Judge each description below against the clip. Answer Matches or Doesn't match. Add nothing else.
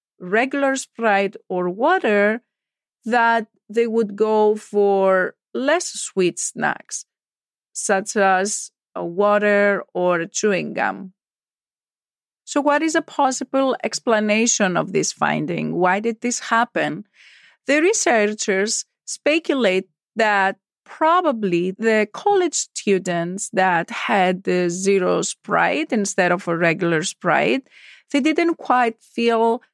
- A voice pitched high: Matches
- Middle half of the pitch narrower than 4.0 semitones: Doesn't match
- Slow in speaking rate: Matches